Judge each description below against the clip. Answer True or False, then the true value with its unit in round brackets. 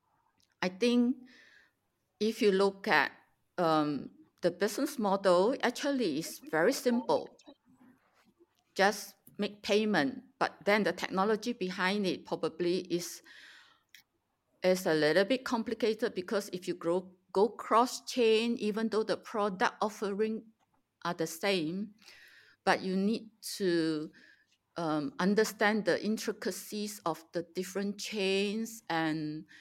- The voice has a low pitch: False (205 Hz)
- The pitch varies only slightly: False (3.8 semitones)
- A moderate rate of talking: False (120 wpm)